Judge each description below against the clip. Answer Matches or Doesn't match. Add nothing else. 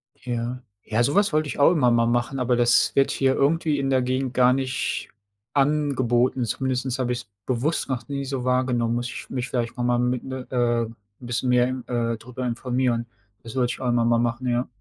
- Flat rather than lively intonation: Matches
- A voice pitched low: Matches